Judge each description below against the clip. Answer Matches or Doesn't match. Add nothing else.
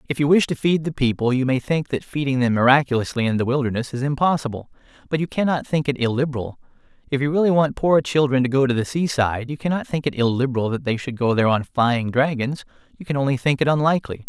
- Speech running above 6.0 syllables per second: Matches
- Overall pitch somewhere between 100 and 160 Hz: Matches